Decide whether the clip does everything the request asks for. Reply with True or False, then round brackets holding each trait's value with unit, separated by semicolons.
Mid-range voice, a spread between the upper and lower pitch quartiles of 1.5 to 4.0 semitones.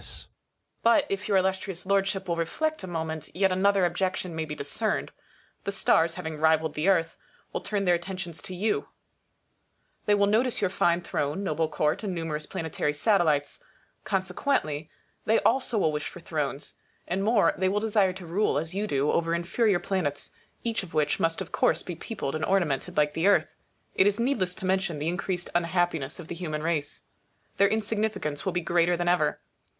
True (180 Hz; 3.6 semitones)